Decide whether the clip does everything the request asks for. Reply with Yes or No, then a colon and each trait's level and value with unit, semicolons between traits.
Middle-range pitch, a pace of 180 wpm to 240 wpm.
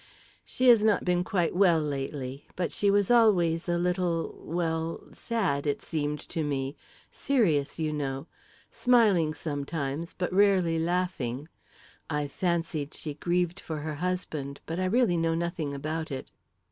No: medium, 165 Hz; average, 145 wpm